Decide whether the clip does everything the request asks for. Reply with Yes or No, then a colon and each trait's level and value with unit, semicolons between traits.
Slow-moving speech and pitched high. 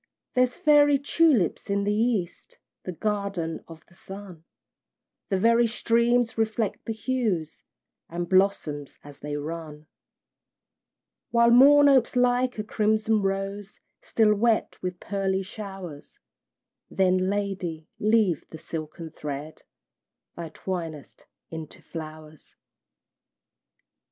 Yes: slow, 110 wpm; high, 195 Hz